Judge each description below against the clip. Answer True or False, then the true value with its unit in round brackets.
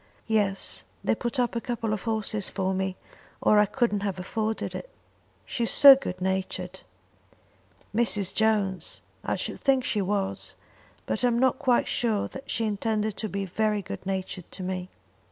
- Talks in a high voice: True (210 Hz)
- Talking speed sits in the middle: True (170 wpm)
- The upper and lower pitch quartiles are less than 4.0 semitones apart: True (3.4 semitones)